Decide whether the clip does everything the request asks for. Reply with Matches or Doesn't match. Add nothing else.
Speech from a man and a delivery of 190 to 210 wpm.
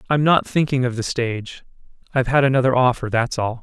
Matches